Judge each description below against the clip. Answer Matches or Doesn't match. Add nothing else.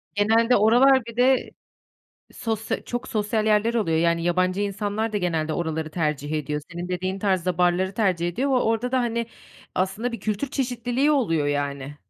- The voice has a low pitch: Doesn't match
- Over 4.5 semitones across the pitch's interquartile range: Matches